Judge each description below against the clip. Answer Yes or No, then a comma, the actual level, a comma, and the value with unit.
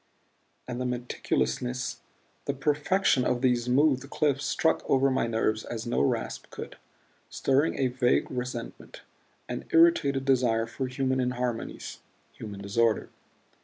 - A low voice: Yes, low, 125 Hz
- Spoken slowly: Yes, slow, 130 wpm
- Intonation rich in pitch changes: No, narrow, 2.4 semitones